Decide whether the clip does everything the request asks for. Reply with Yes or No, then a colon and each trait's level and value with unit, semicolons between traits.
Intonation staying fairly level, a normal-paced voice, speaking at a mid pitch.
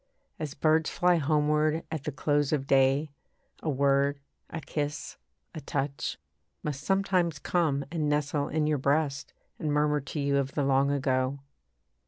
Yes: narrow, 1.9 semitones; average, 155 wpm; medium, 145 Hz